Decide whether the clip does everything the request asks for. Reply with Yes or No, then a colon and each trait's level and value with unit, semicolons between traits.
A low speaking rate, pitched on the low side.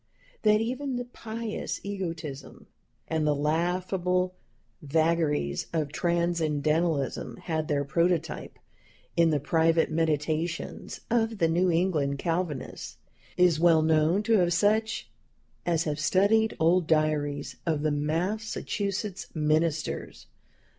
No: slow, 110 wpm; medium, 165 Hz